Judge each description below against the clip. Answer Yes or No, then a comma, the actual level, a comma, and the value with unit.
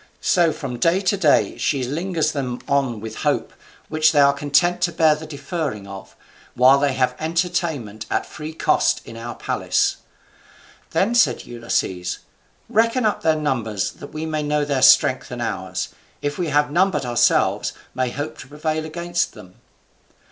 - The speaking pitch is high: No, medium, 150 Hz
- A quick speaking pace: No, average, 170 wpm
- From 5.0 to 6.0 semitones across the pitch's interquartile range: No, average, 4.3 semitones